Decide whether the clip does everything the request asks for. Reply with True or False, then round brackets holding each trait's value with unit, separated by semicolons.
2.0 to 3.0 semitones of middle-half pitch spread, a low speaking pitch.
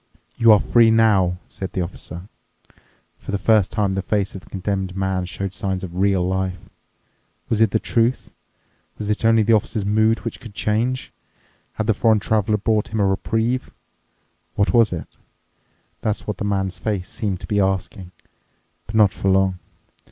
True (2.5 semitones; 100 Hz)